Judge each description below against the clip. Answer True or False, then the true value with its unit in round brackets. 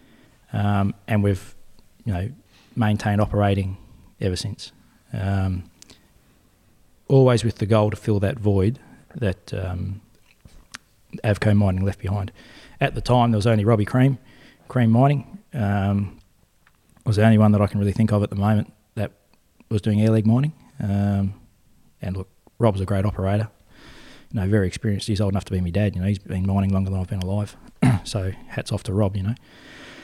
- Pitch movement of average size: False (2.3 semitones)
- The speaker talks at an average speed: True (175 wpm)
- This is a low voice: True (105 Hz)